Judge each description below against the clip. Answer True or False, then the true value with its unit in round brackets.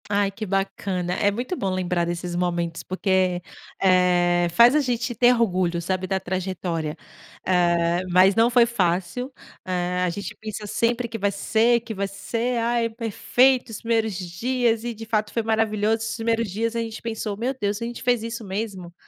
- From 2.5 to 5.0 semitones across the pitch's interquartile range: True (4.1 semitones)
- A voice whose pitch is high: True (205 Hz)